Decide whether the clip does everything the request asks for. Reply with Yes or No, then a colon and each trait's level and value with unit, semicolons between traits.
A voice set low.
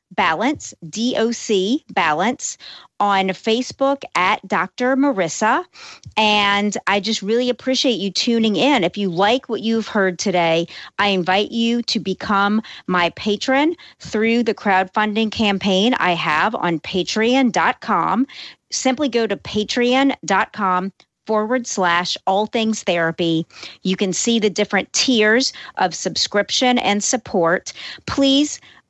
No: high, 215 Hz